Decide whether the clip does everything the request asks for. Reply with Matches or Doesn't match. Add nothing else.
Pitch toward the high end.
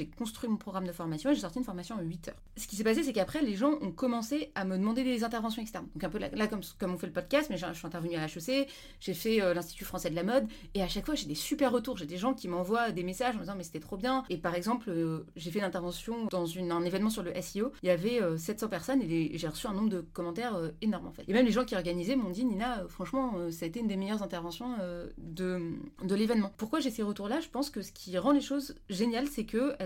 Matches